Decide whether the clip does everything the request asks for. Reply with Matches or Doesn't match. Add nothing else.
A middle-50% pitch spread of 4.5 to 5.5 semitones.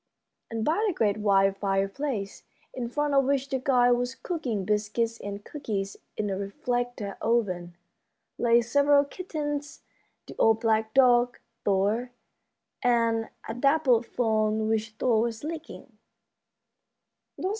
Doesn't match